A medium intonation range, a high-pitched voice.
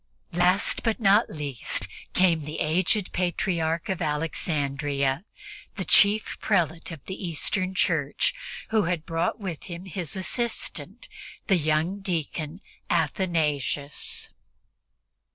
No: average, 3.7 semitones; medium, 170 Hz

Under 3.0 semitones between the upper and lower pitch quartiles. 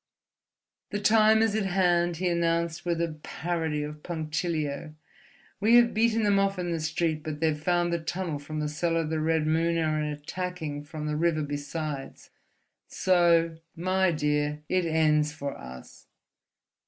Yes: narrow, 2.6 semitones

